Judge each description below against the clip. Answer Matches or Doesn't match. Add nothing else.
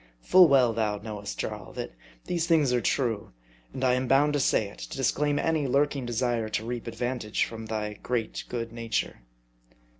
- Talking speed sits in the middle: Matches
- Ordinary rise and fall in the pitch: Matches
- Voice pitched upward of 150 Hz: Doesn't match